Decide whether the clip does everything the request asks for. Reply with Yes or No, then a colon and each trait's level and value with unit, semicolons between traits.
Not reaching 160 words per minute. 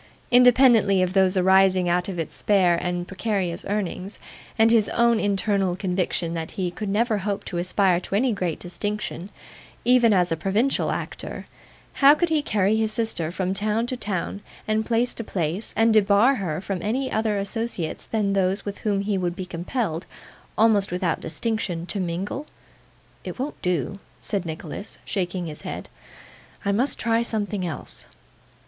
No: average, 165 wpm